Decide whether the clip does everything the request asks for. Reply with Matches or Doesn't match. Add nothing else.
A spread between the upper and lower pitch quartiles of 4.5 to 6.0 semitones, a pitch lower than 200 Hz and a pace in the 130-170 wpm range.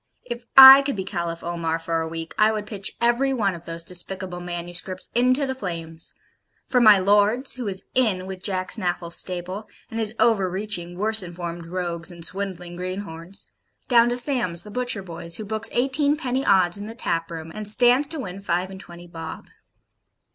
Doesn't match